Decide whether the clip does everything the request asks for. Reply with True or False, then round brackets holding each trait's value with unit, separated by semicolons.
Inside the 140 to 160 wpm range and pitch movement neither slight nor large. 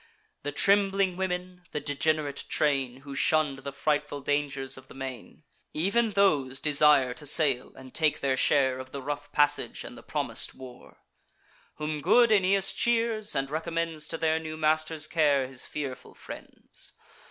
True (155 wpm; 3.3 semitones)